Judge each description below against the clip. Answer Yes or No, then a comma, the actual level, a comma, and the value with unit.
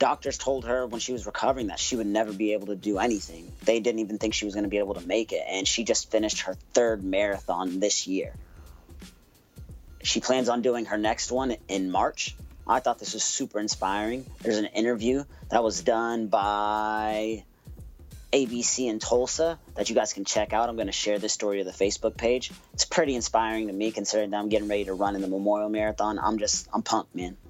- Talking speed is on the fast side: Yes, fast, 220 wpm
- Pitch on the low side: Yes, low, 110 Hz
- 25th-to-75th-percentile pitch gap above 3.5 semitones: No, narrow, 2.4 semitones